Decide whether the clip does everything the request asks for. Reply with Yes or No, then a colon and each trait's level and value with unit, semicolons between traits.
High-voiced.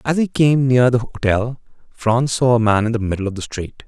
No: low, 120 Hz